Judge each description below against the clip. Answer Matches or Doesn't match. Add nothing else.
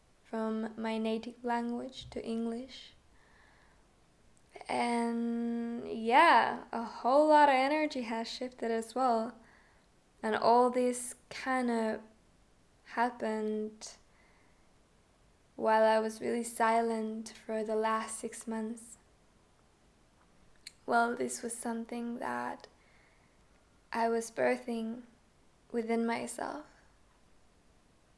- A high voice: Matches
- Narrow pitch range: Matches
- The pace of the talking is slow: Matches